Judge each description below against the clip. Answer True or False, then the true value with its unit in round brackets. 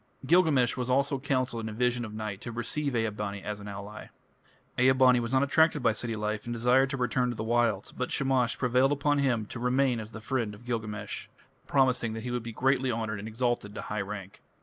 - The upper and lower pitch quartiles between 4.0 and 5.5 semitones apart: False (3.3 semitones)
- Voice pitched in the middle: False (120 Hz)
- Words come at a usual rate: False (225 wpm)